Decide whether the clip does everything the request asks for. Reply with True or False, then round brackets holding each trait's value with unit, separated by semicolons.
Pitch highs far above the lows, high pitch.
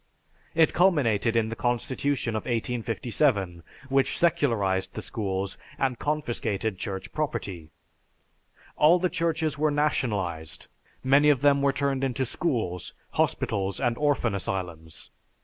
False (6.7 semitones; 120 Hz)